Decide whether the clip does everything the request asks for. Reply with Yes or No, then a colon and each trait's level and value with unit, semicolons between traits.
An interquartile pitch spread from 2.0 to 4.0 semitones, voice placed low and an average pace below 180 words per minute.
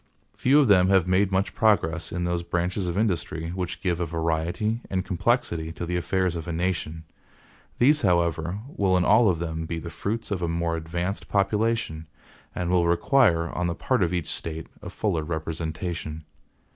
No: average, 2.7 semitones; very low, 85 Hz; average, 185 wpm